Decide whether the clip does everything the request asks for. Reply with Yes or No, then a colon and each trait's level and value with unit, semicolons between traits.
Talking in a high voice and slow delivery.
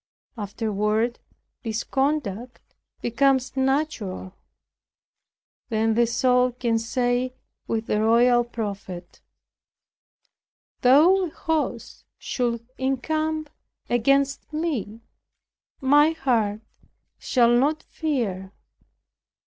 Yes: high, 245 Hz; slow, 80 wpm